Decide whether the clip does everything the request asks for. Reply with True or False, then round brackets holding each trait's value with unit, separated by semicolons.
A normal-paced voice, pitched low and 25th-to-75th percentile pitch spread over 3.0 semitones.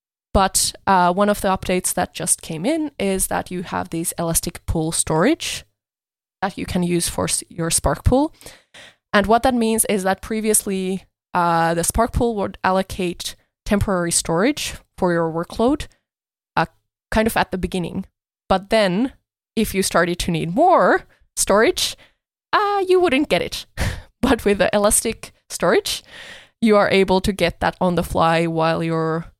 False (165 wpm; 190 Hz; 4.5 semitones)